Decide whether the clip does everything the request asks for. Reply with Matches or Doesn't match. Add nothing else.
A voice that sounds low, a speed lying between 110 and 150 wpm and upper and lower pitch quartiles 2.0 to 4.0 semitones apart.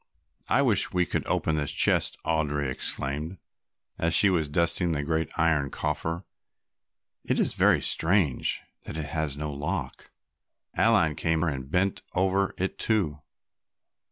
Matches